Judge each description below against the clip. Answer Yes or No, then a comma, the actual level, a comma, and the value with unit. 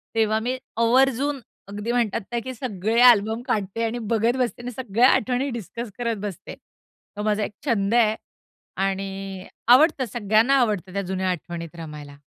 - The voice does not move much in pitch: No, average, 3.7 semitones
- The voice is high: Yes, high, 220 Hz